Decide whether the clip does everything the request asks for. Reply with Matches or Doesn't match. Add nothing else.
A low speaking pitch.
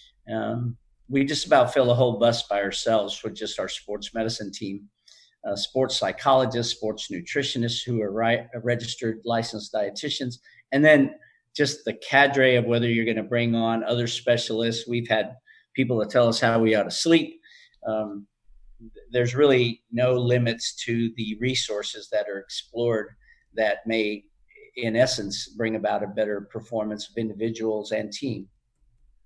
Matches